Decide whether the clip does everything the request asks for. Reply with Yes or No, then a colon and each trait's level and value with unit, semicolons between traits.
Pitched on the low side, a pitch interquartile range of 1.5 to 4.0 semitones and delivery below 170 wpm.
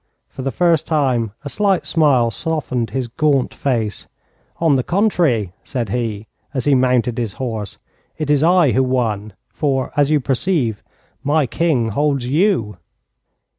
No: low, 130 Hz; average, 4.7 semitones; average, 150 wpm